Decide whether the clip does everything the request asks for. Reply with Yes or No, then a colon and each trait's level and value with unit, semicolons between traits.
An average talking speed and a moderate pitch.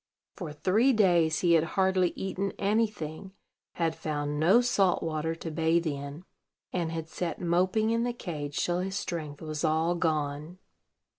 Yes: average, 160 wpm; medium, 170 Hz